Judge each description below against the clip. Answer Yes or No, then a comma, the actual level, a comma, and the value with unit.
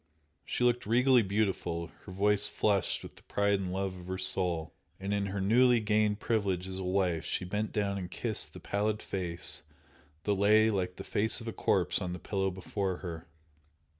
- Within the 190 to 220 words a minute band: Yes, average, 195 wpm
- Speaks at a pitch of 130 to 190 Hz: No, low, 100 Hz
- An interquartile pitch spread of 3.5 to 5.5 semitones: No, narrow, 2.4 semitones